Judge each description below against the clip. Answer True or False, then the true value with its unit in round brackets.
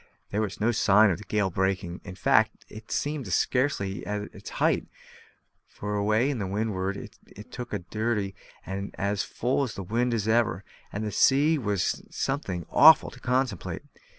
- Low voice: True (105 Hz)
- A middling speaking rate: True (175 wpm)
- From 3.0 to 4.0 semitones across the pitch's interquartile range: True (3.7 semitones)